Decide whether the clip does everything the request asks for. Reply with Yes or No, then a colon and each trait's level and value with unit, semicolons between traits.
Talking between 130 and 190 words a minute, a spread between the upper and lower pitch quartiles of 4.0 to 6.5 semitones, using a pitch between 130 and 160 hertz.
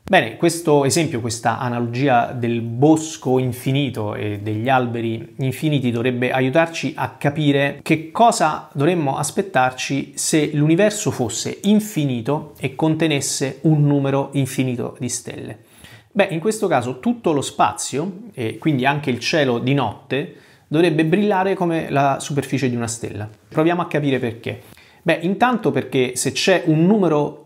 Yes: average, 140 wpm; average, 4.3 semitones; medium, 140 Hz